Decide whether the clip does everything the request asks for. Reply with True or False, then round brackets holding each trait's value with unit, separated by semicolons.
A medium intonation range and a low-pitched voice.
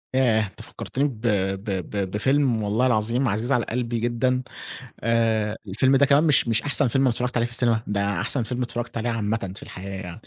True (3.2 semitones; 115 Hz)